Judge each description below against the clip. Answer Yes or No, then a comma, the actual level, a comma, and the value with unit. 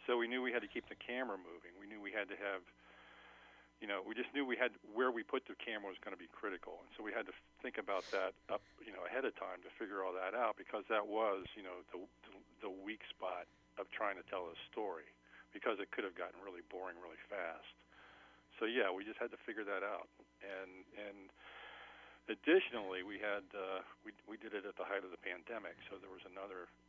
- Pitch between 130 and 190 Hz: No, low, 105 Hz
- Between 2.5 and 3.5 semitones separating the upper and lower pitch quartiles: No, average, 4.3 semitones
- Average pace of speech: No, fast, 235 wpm